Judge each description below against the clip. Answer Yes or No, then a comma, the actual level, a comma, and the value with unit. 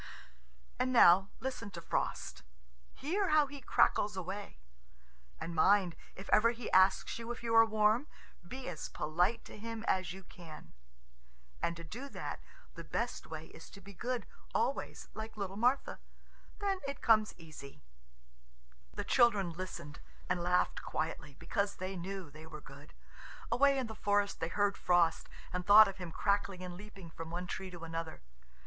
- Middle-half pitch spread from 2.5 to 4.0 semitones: No, average, 4.9 semitones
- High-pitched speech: Yes, high, 195 Hz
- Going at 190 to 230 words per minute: No, average, 165 wpm